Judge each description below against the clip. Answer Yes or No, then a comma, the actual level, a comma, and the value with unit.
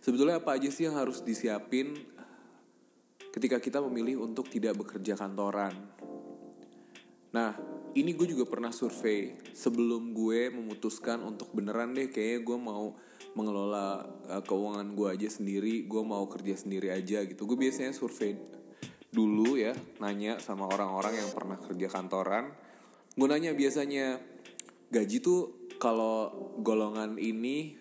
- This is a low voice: Yes, low, 110 Hz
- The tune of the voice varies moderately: Yes, average, 4.3 semitones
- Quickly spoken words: No, average, 130 wpm